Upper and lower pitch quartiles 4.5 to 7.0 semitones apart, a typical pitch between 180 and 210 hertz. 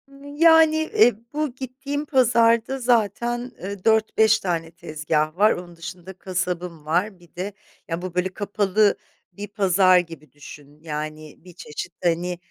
Yes: average, 5.3 semitones; medium, 185 Hz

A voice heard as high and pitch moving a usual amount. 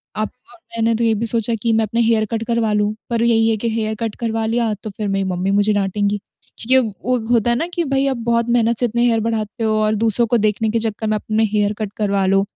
No: high, 225 Hz; narrow, 1.7 semitones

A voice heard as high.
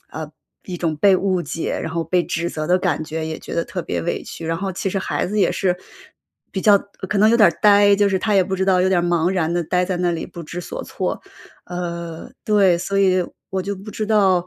No: medium, 180 Hz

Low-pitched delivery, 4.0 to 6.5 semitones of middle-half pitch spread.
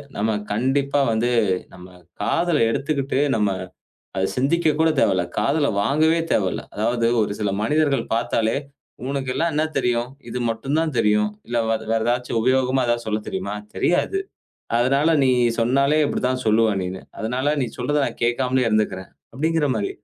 Yes: low, 125 Hz; average, 4.4 semitones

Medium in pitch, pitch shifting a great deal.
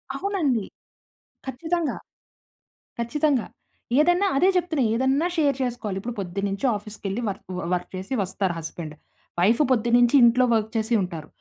No: high, 235 Hz; wide, 6.5 semitones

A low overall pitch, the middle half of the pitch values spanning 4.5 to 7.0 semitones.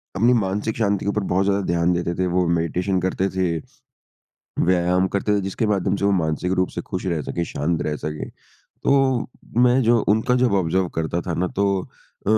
No: very low, 95 Hz; average, 2.8 semitones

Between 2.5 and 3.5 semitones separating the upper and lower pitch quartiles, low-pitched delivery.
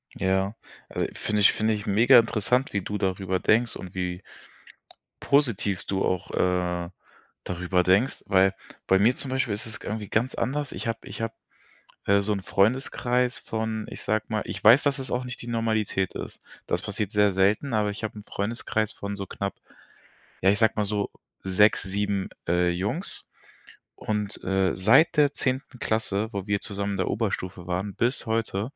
Yes: average, 2.9 semitones; low, 105 Hz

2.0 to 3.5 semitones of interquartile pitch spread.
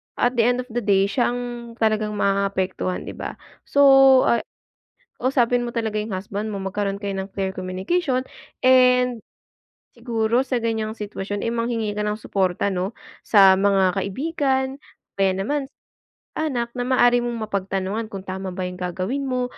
No: average, 3.9 semitones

